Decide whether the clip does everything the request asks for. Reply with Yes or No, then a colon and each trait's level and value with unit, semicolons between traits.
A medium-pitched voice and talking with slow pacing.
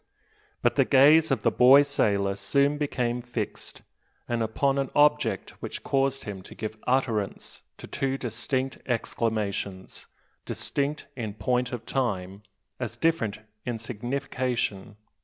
No: low, 125 Hz; slow, 130 wpm